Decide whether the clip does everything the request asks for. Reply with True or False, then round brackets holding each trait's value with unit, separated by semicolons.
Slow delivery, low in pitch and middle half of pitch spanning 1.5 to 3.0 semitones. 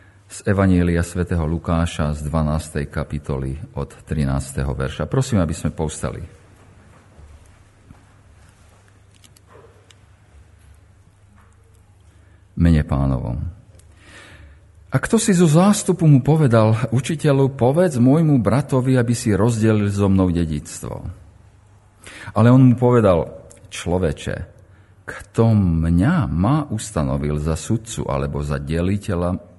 False (95 wpm; 95 Hz; 4.6 semitones)